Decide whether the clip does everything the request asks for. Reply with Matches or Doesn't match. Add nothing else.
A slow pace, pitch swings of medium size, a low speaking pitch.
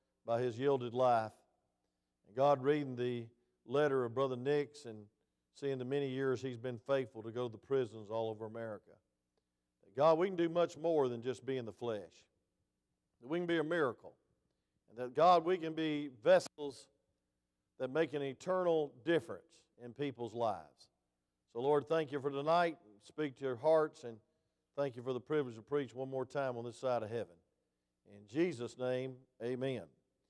Doesn't match